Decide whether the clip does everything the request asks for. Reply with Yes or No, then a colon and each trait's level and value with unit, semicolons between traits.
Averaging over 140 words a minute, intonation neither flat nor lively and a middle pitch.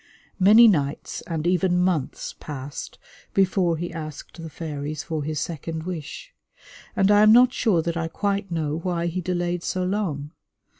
Yes: average, 160 wpm; average, 3.2 semitones; medium, 170 Hz